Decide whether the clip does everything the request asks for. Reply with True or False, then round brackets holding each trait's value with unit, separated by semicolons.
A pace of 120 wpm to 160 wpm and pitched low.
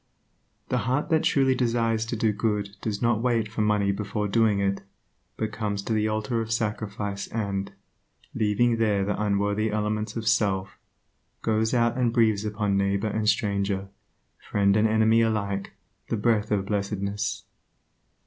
True (155 wpm; 105 Hz)